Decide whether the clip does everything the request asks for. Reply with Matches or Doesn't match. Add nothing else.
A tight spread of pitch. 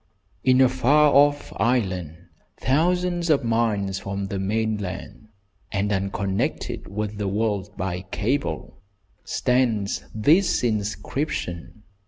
Doesn't match